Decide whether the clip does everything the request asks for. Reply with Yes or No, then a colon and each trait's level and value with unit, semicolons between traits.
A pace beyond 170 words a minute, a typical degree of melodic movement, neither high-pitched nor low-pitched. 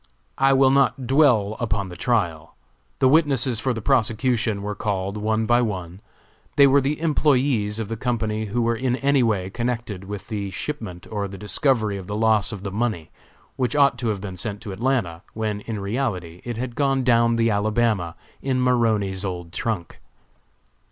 No: average, 180 wpm; average, 3.9 semitones; low, 110 Hz